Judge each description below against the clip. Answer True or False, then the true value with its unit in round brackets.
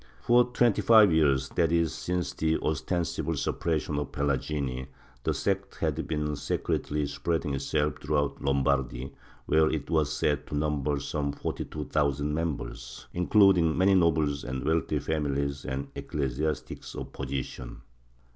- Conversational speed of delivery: True (145 wpm)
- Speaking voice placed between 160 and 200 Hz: False (75 Hz)